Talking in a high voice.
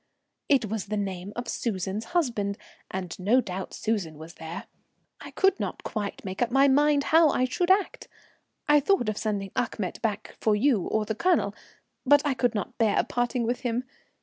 Yes: high, 225 Hz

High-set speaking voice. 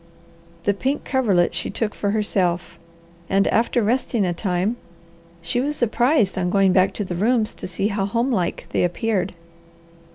Yes: high, 205 Hz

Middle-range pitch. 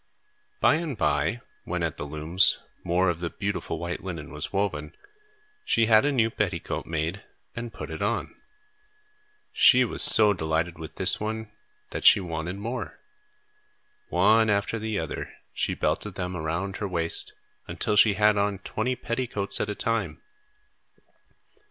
No: low, 100 Hz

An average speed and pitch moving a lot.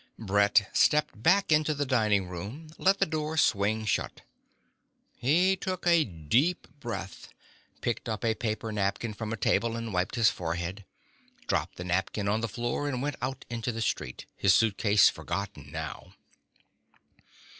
Yes: average, 155 wpm; wide, 6.2 semitones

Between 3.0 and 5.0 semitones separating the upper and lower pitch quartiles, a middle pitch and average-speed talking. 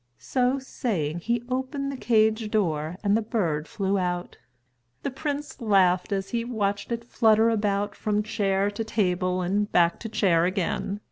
No: average, 3.8 semitones; high, 205 Hz; average, 160 wpm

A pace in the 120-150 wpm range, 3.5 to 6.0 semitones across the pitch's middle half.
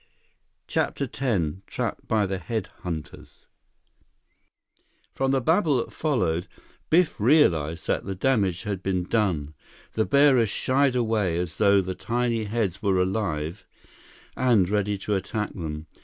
Yes: slow, 135 wpm; average, 5.2 semitones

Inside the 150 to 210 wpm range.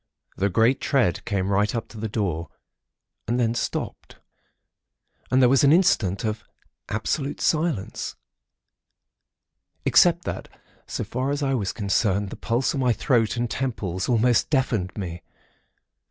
No: average, 140 wpm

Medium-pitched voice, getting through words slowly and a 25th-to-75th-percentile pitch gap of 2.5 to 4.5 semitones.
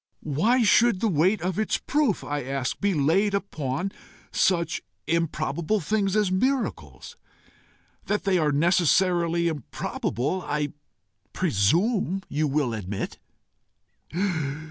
No: medium, 175 Hz; slow, 110 wpm; average, 5.3 semitones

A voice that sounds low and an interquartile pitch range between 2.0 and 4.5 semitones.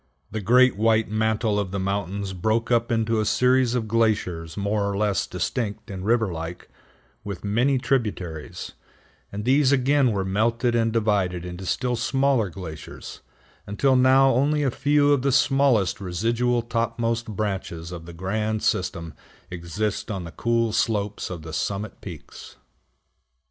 Yes: low, 110 Hz; average, 3.8 semitones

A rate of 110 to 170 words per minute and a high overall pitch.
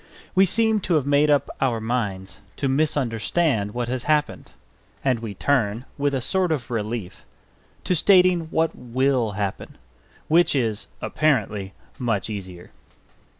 No: average, 140 wpm; low, 130 Hz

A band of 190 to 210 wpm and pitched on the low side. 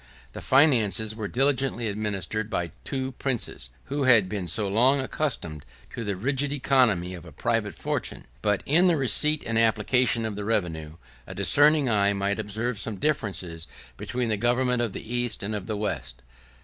No: average, 175 wpm; low, 110 Hz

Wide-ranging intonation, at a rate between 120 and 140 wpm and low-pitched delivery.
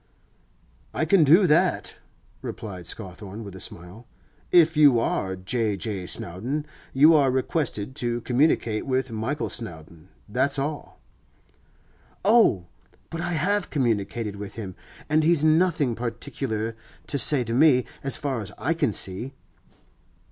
Yes: wide, 6.4 semitones; slow, 135 wpm; low, 125 Hz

